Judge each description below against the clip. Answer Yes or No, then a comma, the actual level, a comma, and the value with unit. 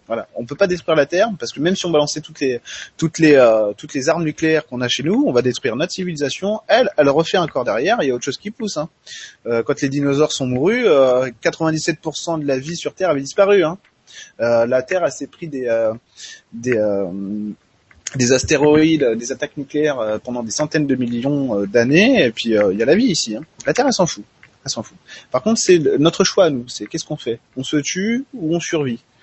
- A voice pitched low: No, medium, 145 Hz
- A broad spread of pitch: No, average, 5.0 semitones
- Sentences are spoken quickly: Yes, fast, 245 wpm